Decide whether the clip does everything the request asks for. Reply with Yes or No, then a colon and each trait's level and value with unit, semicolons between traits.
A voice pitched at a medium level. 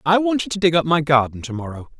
Yes: medium, 155 Hz